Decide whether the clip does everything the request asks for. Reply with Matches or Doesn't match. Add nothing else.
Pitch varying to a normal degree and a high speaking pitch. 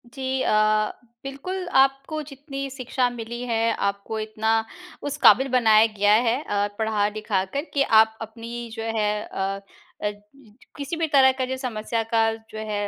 Matches